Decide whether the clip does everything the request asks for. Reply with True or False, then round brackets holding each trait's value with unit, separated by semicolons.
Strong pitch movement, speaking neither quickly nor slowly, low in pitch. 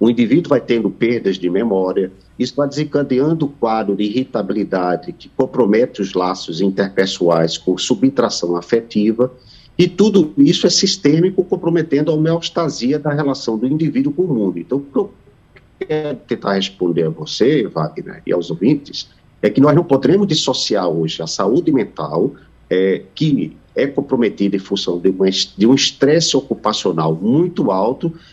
True (7.9 semitones; 155 wpm; 125 Hz)